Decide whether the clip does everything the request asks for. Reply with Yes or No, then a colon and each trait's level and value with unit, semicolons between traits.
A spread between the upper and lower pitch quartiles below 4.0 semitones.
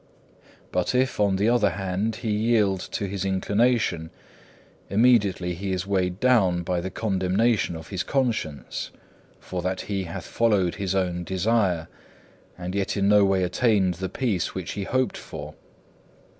Yes: average, 3.1 semitones